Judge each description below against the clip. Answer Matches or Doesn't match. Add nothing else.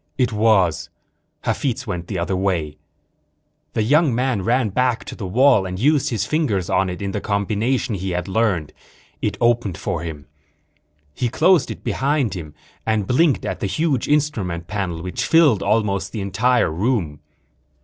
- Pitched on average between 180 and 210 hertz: Doesn't match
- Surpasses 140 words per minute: Matches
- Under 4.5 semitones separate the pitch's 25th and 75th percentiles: Doesn't match